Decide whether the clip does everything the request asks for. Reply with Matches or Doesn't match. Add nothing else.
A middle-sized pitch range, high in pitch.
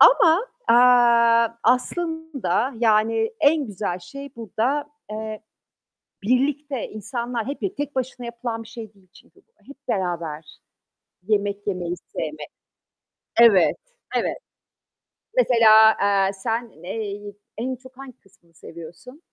Matches